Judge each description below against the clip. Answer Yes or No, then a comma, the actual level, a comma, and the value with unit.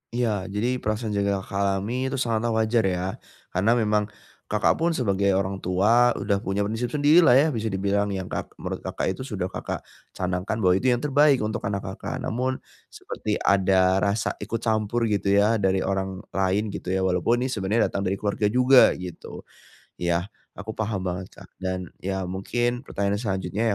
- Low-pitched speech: Yes, low, 100 Hz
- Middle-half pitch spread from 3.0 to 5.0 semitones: Yes, average, 3.5 semitones